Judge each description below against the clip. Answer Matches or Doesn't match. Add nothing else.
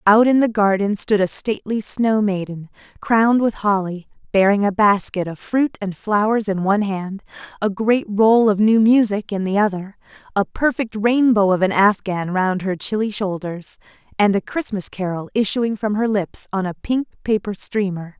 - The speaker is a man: Doesn't match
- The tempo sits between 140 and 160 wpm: Doesn't match